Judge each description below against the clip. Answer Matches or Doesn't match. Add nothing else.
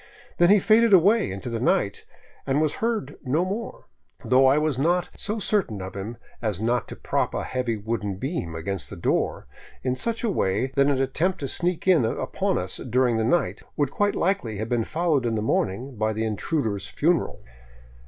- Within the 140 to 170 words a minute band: Doesn't match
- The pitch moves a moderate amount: Doesn't match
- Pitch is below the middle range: Matches